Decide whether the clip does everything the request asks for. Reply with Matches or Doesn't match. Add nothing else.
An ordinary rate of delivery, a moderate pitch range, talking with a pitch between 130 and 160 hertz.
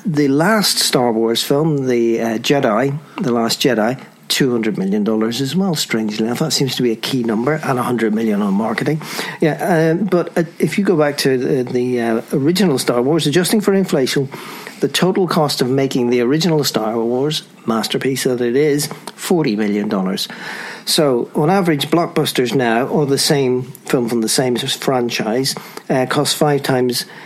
Doesn't match